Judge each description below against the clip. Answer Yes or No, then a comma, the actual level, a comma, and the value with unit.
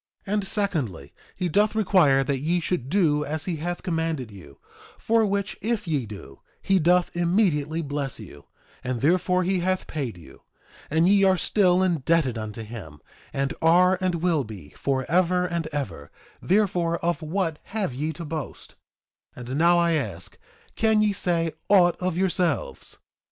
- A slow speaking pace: No, average, 165 wpm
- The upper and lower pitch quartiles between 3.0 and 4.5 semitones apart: No, average, 5.1 semitones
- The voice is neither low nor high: Yes, medium, 165 Hz